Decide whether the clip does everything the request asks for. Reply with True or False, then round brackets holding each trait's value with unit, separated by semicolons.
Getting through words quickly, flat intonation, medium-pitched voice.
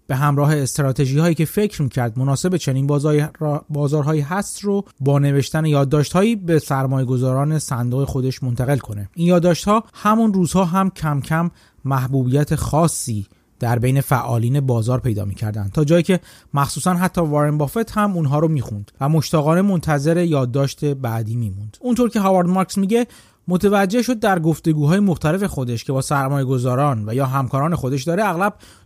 False (170 wpm; 4.8 semitones; 145 Hz)